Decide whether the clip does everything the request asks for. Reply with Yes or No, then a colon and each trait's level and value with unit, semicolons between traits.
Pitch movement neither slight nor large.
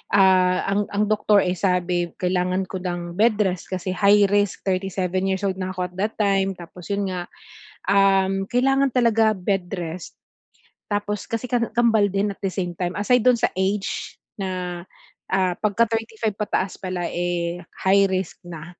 No: narrow, 2.3 semitones